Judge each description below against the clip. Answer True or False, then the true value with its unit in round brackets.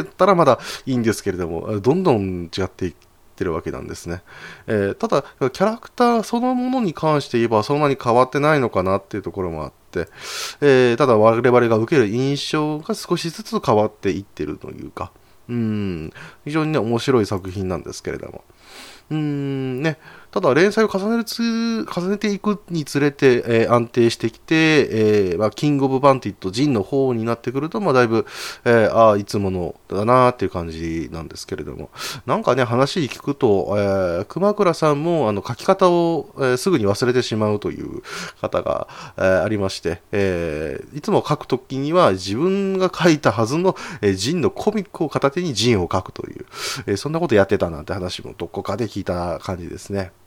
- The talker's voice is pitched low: True (125 Hz)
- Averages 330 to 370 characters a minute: False (395 characters per minute)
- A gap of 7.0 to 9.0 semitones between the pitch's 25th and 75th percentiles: True (7.8 semitones)